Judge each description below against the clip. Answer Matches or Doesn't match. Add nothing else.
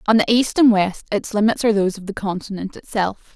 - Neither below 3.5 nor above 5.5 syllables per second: Doesn't match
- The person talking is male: Doesn't match